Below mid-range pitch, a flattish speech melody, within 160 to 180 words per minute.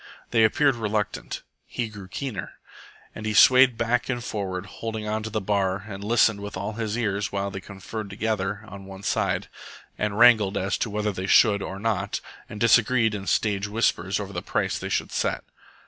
No: low, 105 Hz; narrow, 2.3 semitones; average, 190 wpm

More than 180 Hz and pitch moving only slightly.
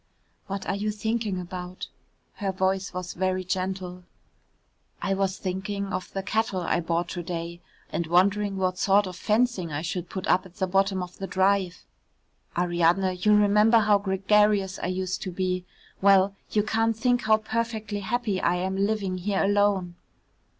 Yes: high, 190 Hz; narrow, 2.2 semitones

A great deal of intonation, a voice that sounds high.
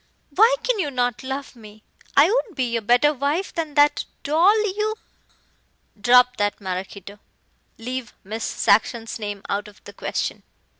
Yes: wide, 6.1 semitones; very high, 250 Hz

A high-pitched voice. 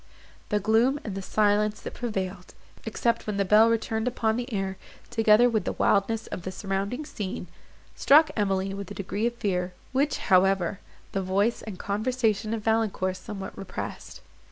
Yes: high, 210 Hz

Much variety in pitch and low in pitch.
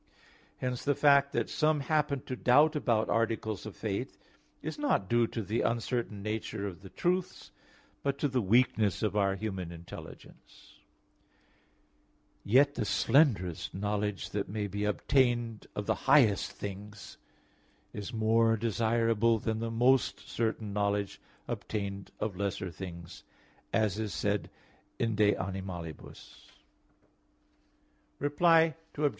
No: average, 3.9 semitones; low, 110 Hz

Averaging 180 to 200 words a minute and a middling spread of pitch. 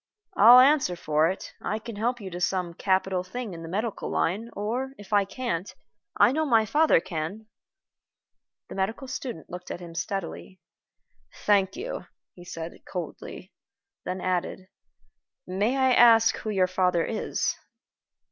No: average, 150 wpm; average, 4.4 semitones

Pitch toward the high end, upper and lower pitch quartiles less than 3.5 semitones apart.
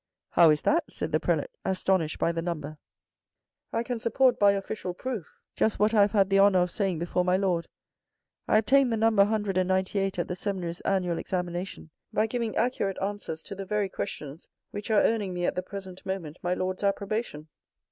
Yes: high, 195 Hz; average, 3.0 semitones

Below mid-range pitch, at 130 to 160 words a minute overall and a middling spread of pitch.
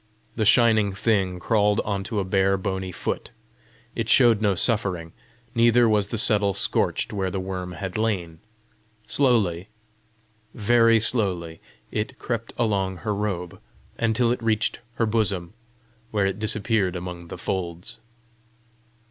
Yes: low, 100 Hz; slow, 135 wpm; average, 3.3 semitones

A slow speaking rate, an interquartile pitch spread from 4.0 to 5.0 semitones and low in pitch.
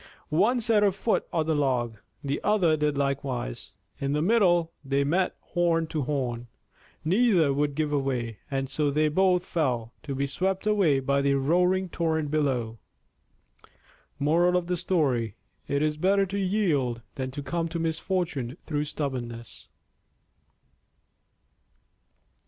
No: slow, 130 wpm; average, 4.6 semitones; medium, 150 Hz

